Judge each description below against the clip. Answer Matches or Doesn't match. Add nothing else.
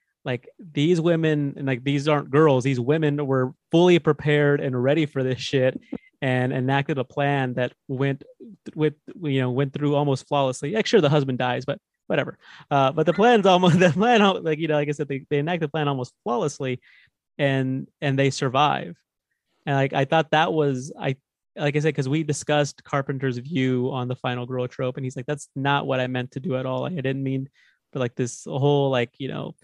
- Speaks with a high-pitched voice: Doesn't match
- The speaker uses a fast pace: Matches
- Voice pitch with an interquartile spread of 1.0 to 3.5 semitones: Matches